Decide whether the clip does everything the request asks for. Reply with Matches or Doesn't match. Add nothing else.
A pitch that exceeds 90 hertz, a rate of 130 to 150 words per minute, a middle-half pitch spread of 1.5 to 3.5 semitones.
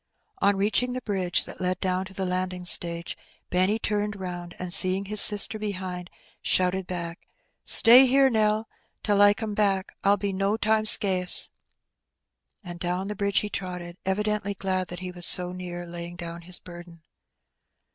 Doesn't match